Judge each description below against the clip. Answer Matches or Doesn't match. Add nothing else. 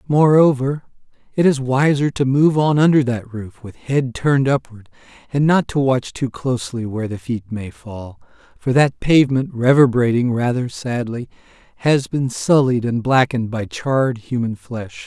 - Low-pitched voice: Matches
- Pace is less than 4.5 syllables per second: Doesn't match